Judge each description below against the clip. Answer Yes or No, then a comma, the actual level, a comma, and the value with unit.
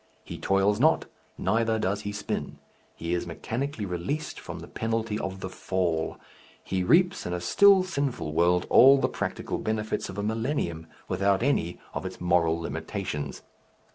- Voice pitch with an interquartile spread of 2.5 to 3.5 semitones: No, average, 4.7 semitones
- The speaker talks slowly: No, average, 160 wpm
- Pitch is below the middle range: Yes, low, 100 Hz